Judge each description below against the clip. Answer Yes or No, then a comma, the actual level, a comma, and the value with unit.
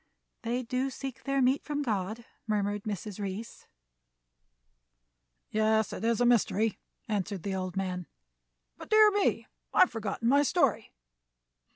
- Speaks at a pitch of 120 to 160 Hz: No, high, 225 Hz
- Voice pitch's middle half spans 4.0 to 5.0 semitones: Yes, average, 4.3 semitones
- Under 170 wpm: Yes, average, 140 wpm